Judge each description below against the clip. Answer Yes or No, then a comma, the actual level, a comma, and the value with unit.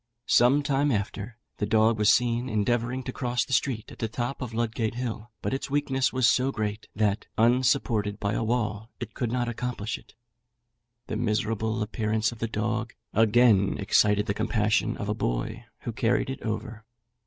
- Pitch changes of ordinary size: No, narrow, 2.3 semitones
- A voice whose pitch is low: Yes, low, 115 Hz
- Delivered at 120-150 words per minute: No, average, 175 wpm